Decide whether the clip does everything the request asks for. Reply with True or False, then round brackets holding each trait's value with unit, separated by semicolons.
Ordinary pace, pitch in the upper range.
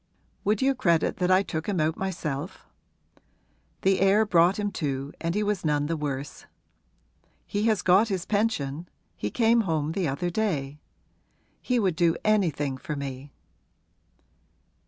False (150 wpm; 175 Hz)